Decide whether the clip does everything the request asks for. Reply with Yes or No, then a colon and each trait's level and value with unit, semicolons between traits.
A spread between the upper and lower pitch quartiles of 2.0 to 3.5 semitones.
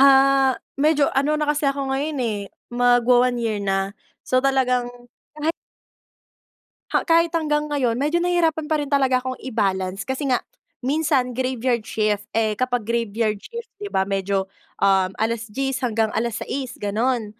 No: average, 4.3 semitones